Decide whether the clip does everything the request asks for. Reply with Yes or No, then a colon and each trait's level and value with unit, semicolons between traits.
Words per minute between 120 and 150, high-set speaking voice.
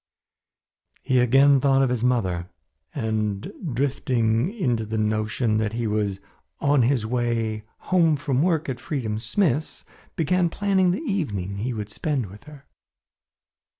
No: average, 140 wpm; low, 125 Hz